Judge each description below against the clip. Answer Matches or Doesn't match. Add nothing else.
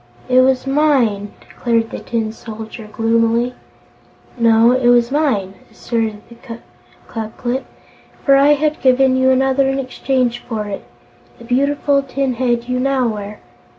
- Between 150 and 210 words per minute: Doesn't match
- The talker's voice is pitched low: Doesn't match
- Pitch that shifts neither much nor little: Matches